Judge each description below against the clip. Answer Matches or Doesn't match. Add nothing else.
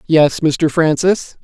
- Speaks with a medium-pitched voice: Matches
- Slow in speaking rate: Matches